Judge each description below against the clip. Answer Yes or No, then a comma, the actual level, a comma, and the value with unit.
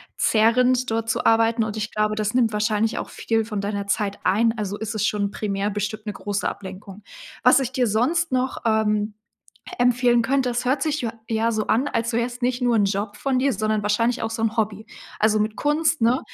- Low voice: No, high, 225 Hz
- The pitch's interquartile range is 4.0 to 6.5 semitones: No, narrow, 2.6 semitones